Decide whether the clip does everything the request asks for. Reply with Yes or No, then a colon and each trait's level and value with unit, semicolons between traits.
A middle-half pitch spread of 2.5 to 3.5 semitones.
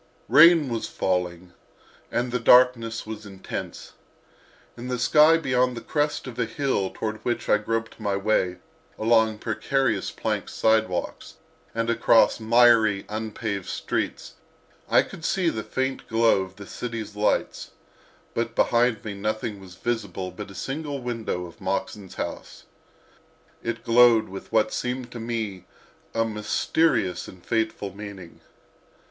Yes: average, 3.1 semitones